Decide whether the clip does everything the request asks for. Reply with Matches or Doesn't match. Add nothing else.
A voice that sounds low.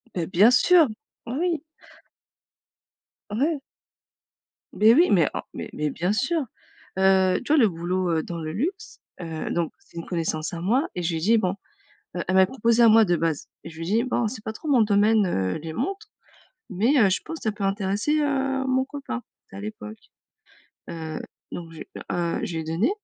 Doesn't match